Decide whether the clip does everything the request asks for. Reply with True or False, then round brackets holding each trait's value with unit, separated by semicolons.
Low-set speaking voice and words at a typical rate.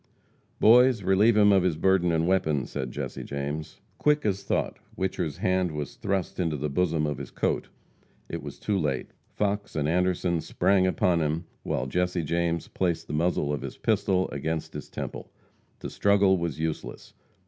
True (90 Hz; 170 wpm)